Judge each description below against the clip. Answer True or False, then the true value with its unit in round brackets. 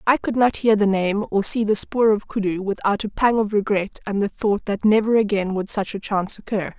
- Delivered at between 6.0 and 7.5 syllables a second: False (5.3 syllables/s)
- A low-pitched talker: False (205 Hz)